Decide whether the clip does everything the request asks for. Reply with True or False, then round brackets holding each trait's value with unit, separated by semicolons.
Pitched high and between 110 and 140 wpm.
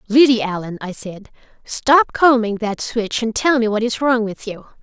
False (230 Hz; 200 wpm)